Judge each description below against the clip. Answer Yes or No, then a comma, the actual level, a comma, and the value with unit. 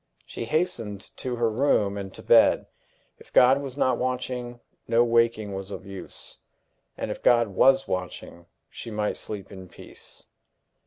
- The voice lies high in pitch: No, low, 115 Hz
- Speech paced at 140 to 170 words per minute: Yes, average, 155 wpm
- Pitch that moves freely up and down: No, average, 4.1 semitones